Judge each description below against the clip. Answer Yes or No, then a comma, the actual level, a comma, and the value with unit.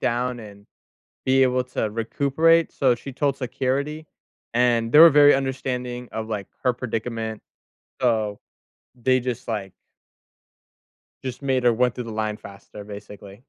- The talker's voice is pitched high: No, low, 125 Hz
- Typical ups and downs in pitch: Yes, average, 3.1 semitones